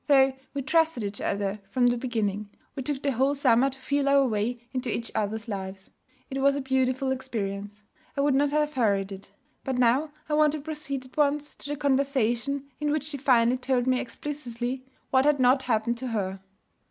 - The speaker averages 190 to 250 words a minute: Yes, average, 200 wpm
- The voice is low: No, very high, 260 Hz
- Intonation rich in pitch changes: No, average, 3.4 semitones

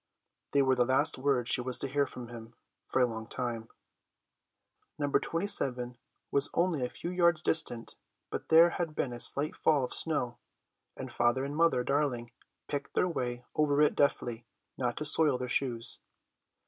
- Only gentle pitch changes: No, average, 3.7 semitones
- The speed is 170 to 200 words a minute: Yes, average, 175 wpm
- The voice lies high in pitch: No, low, 130 Hz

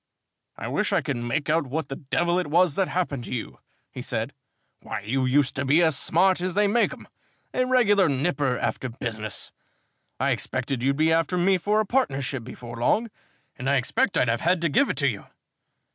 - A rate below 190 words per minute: No, fast, 205 wpm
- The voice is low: No, medium, 150 Hz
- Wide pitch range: Yes, wide, 6.0 semitones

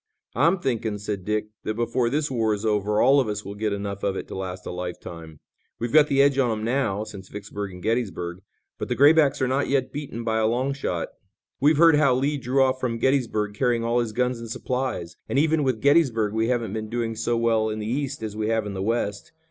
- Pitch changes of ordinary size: Yes, average, 4.1 semitones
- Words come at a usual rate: No, fast, 235 wpm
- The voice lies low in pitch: Yes, low, 115 Hz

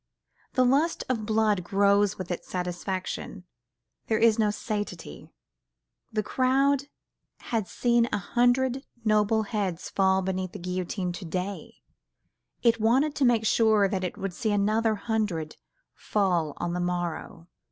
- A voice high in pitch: Yes, high, 205 Hz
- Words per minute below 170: Yes, average, 140 wpm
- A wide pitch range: No, average, 3.8 semitones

